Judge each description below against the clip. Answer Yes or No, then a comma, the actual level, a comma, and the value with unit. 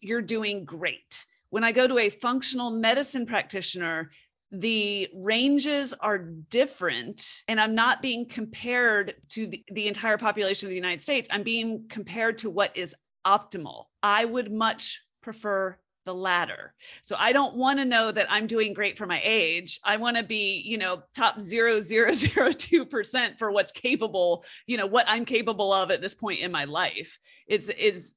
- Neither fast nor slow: Yes, average, 175 wpm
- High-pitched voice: Yes, high, 215 Hz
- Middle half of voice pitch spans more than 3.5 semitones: No, average, 3.2 semitones